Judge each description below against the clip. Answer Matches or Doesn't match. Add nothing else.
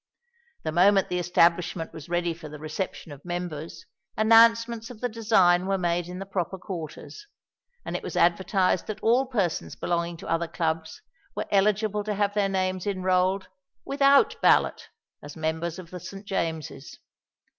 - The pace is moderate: Matches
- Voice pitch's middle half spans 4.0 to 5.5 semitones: Doesn't match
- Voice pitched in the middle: Matches